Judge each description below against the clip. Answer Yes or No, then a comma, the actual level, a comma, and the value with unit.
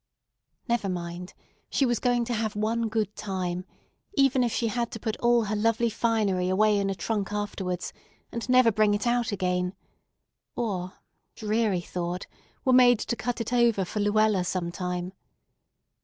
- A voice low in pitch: No, high, 215 Hz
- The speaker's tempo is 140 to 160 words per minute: Yes, average, 155 wpm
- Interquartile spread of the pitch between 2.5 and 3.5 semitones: No, average, 4.0 semitones